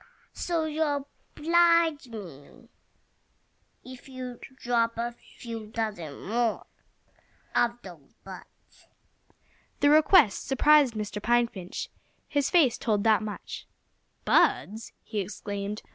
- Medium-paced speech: No, slow, 105 wpm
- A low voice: No, high, 235 Hz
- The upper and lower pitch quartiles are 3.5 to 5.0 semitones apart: No, wide, 5.4 semitones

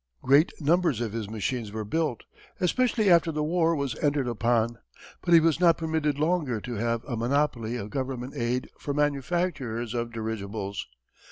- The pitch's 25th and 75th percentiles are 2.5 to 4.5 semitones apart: No, wide, 5.5 semitones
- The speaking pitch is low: Yes, low, 130 Hz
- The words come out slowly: No, average, 165 wpm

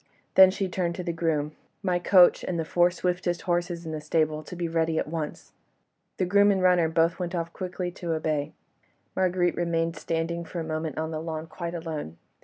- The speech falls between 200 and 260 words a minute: Yes, fast, 205 wpm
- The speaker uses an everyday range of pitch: No, narrow, 1.9 semitones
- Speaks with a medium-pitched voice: Yes, medium, 170 Hz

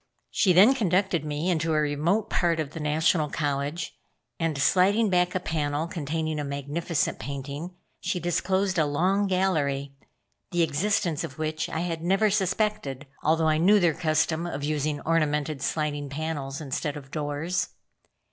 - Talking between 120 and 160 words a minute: Yes, average, 155 wpm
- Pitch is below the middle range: No, medium, 160 Hz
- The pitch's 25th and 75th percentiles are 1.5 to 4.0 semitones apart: Yes, average, 3.5 semitones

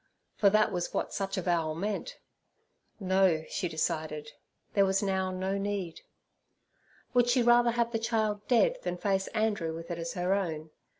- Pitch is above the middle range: Yes, high, 195 Hz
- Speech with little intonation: No, average, 3.8 semitones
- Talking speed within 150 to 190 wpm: Yes, average, 165 wpm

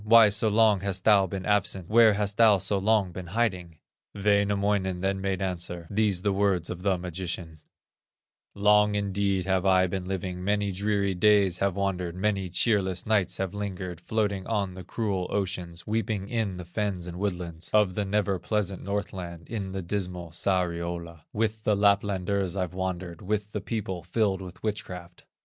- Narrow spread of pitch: Yes, narrow, 2.3 semitones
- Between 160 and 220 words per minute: Yes, average, 165 wpm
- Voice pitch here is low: Yes, very low, 95 Hz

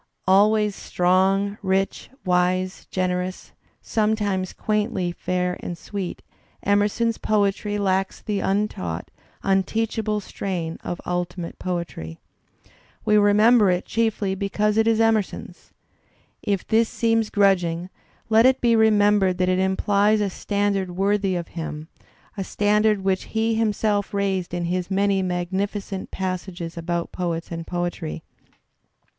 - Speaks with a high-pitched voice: Yes, high, 195 Hz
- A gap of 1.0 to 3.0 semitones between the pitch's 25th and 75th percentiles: Yes, narrow, 2.6 semitones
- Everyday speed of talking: No, slow, 125 wpm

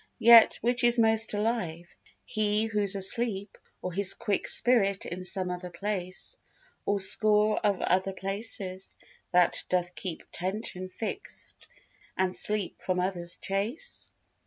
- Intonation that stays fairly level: No, average, 3.1 semitones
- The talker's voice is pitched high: Yes, high, 200 Hz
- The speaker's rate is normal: No, slow, 130 wpm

